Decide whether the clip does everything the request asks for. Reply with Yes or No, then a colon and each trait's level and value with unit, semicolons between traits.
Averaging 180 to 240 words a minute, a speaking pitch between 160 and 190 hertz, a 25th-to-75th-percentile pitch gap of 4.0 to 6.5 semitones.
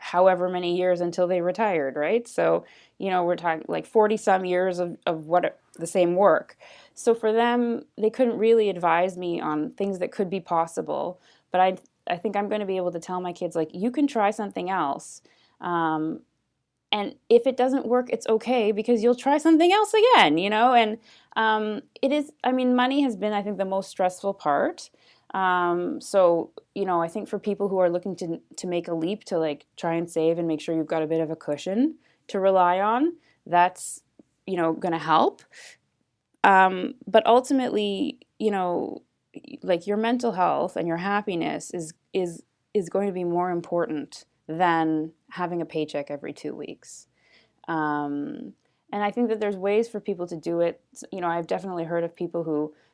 Yes: average, 195 wpm; medium, 185 Hz; average, 4.3 semitones